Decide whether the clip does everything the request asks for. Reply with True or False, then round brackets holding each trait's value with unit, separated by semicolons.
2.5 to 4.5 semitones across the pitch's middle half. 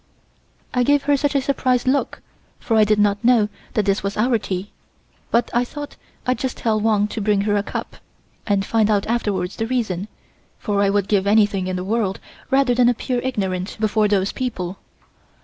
True (3.5 semitones)